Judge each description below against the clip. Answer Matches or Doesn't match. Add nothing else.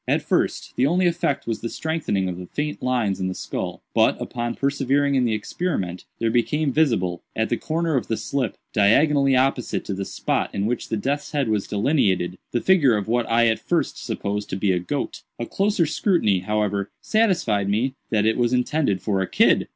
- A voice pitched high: Doesn't match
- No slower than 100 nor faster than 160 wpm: Doesn't match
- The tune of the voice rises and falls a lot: Matches